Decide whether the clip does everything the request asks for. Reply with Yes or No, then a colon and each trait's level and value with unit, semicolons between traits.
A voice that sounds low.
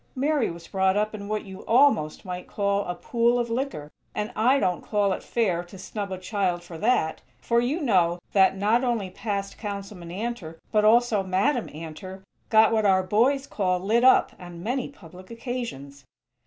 No: high, 205 Hz